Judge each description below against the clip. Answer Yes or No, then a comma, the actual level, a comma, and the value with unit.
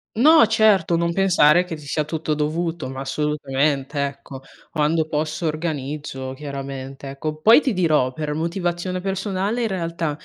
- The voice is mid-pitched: Yes, medium, 155 Hz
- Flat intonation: No, average, 3.6 semitones